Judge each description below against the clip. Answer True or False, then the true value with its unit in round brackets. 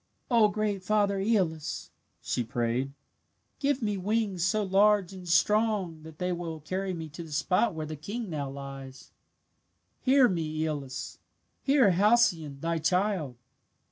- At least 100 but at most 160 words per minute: True (140 wpm)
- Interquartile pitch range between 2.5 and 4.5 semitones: False (5.2 semitones)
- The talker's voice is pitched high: False (180 Hz)